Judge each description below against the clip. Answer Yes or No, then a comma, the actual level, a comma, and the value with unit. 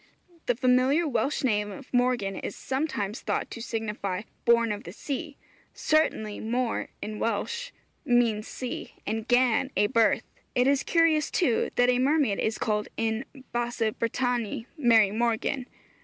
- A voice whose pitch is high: Yes, high, 240 Hz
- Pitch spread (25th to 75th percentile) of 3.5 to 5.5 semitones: No, average, 3.1 semitones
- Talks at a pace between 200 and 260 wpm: No, average, 145 wpm